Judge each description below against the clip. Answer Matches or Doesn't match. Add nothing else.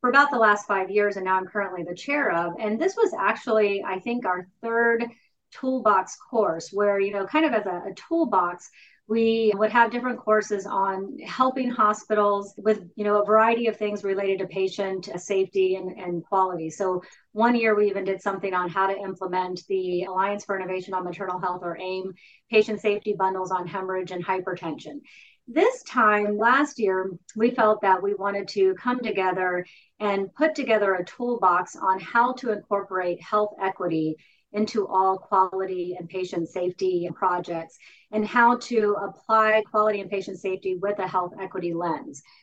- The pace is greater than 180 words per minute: Doesn't match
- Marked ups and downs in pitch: Doesn't match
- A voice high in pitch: Matches